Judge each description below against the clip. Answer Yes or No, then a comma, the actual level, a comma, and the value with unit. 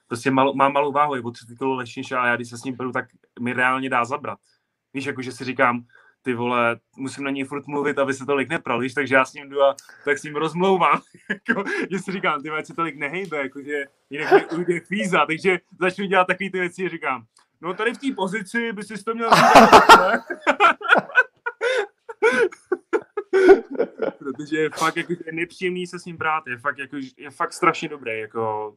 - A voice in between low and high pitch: Yes, medium, 150 Hz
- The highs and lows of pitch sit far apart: Yes, wide, 6.1 semitones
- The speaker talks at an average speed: No, fast, 200 wpm